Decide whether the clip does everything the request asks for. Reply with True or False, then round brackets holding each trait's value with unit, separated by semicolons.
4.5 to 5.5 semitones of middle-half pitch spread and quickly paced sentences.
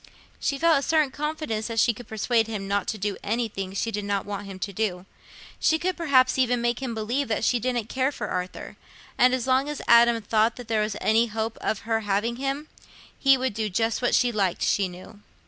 False (3.7 semitones; 220 wpm)